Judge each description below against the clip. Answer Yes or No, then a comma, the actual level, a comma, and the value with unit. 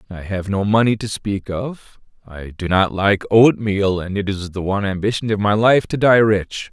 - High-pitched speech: No, low, 100 Hz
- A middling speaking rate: No, fast, 215 wpm